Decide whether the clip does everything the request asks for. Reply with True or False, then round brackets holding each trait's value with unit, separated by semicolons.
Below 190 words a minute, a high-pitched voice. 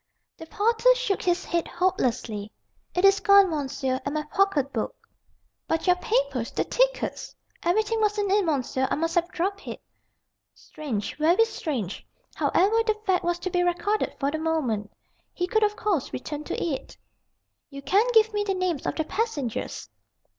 True (175 wpm; 350 Hz)